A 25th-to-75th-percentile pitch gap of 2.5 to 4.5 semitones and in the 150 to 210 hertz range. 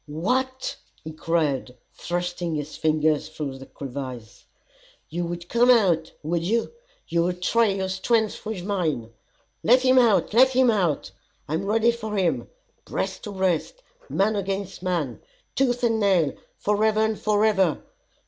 No: wide, 5.5 semitones; high, 190 Hz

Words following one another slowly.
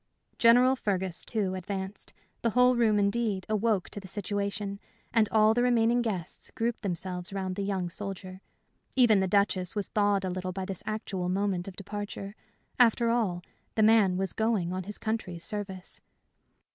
No: average, 165 wpm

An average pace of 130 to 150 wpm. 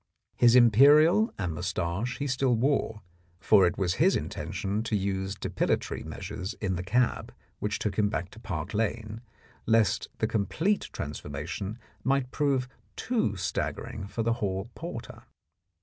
Yes: average, 145 wpm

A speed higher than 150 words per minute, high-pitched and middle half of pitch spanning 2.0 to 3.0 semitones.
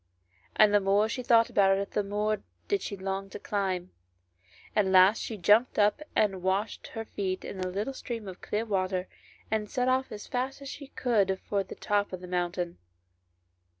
Yes: average, 195 wpm; high, 205 Hz; average, 2.7 semitones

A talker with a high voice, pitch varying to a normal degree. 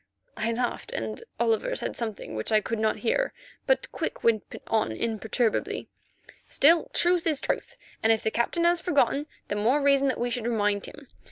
Yes: high, 235 Hz; average, 4.7 semitones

